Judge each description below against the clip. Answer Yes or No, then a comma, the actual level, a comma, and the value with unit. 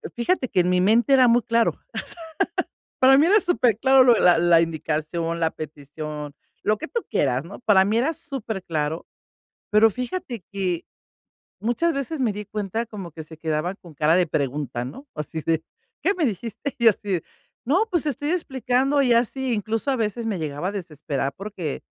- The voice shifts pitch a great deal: Yes, wide, 7.7 semitones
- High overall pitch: Yes, high, 210 Hz